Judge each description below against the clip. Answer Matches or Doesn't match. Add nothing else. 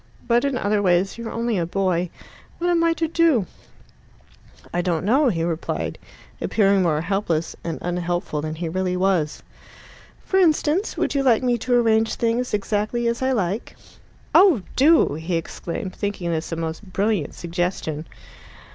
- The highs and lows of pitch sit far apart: Matches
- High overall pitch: Matches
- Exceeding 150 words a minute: Matches